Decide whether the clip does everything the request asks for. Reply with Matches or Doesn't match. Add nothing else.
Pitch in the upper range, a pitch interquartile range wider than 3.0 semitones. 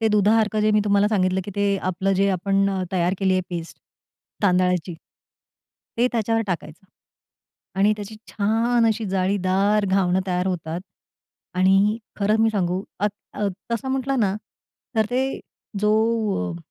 Doesn't match